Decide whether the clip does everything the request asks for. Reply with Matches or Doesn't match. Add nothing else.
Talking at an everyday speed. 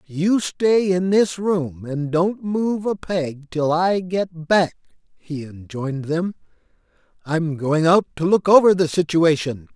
Matches